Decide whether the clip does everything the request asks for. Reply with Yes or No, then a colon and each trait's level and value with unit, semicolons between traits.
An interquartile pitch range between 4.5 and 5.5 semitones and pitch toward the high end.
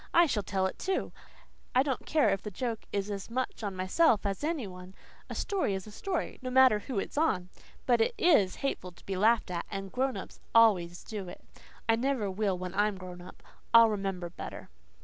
Yes: average, 5.2 semitones; high, 210 Hz